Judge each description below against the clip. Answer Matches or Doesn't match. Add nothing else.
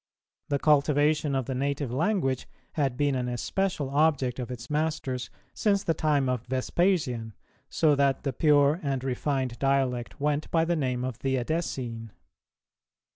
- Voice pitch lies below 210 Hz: Matches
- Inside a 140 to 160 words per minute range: Matches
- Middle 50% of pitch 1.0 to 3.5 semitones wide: Matches